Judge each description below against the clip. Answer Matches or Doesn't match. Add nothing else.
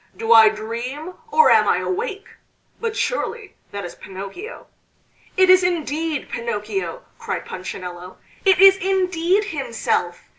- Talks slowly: Matches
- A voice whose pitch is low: Doesn't match